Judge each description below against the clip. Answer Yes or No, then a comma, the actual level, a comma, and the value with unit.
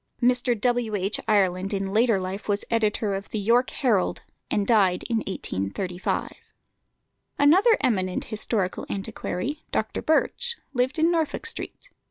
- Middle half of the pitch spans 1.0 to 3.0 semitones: No, average, 4.3 semitones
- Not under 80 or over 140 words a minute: Yes, slow, 135 wpm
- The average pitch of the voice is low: No, high, 215 Hz